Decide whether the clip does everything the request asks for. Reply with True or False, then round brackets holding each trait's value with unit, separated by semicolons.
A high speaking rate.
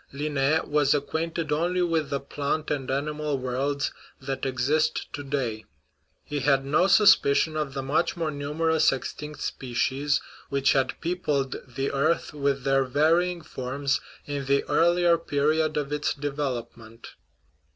False (140 wpm)